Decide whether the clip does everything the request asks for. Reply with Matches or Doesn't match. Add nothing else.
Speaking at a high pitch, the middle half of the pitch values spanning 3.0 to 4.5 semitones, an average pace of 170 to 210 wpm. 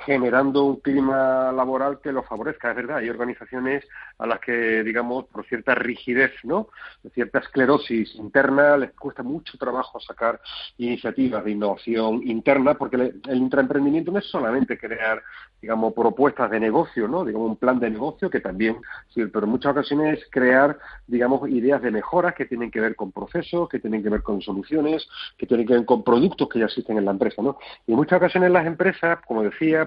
Doesn't match